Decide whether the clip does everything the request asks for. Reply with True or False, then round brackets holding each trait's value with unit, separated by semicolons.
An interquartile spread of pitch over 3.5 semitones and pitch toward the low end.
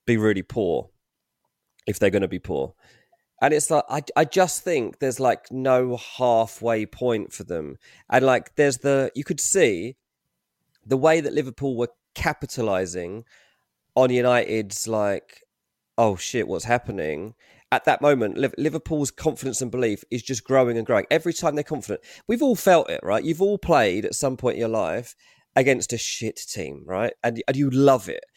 True (4.7 semitones; 130 Hz)